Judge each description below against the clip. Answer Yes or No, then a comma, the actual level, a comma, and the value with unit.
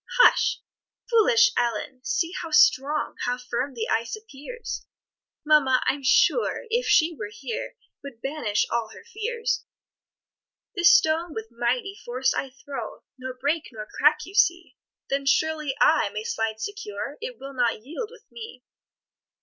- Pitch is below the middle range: No, very high, 285 Hz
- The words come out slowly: No, average, 150 wpm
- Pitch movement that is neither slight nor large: No, wide, 8.4 semitones